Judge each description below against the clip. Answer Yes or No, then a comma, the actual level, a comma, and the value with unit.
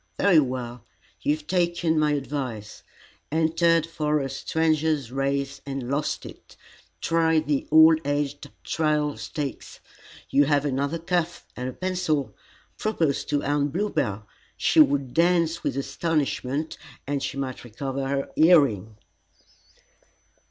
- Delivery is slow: Yes, slow, 125 wpm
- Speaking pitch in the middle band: Yes, medium, 145 Hz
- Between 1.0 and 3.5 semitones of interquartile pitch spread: Yes, average, 2.9 semitones